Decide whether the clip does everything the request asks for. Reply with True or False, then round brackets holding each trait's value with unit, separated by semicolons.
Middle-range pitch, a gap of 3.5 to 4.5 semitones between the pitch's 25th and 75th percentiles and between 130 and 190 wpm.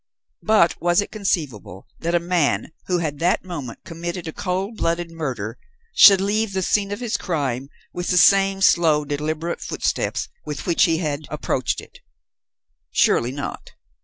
True (170 Hz; 4.2 semitones; 160 wpm)